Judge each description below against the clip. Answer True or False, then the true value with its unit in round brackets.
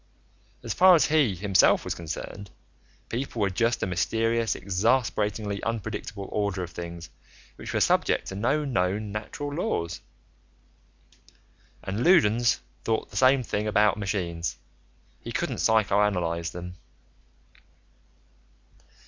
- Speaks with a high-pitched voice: False (105 Hz)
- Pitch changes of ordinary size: True (4.1 semitones)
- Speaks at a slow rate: True (115 wpm)